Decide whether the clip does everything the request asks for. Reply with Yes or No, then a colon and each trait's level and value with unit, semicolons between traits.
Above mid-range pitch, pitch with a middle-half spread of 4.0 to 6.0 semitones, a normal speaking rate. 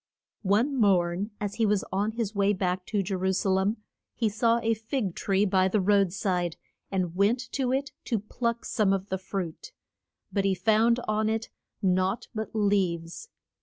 No: high, 200 Hz; average, 2.8 semitones; average, 180 wpm